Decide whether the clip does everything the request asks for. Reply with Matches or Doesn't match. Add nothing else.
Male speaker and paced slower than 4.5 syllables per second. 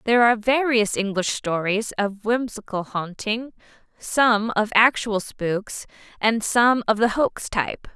Doesn't match